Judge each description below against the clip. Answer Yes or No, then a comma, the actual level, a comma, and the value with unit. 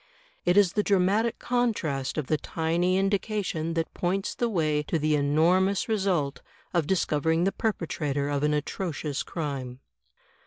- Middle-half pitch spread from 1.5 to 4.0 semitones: No, average, 4.6 semitones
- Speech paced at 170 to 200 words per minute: No, average, 145 wpm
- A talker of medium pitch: Yes, medium, 165 Hz